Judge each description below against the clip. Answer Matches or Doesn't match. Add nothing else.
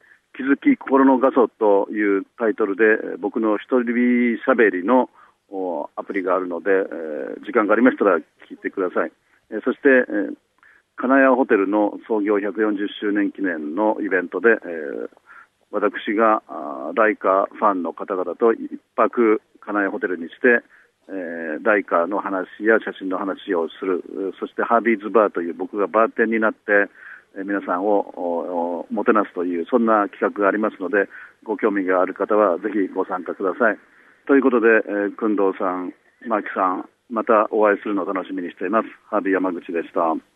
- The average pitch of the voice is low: Matches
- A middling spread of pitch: Matches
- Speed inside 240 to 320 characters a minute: Matches